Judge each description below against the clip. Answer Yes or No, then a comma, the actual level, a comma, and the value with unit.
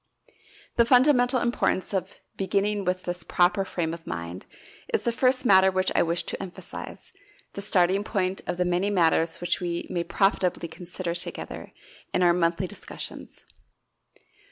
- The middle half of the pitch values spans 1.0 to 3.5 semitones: Yes, narrow, 2.6 semitones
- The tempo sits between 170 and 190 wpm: No, average, 155 wpm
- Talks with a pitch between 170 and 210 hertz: Yes, medium, 185 Hz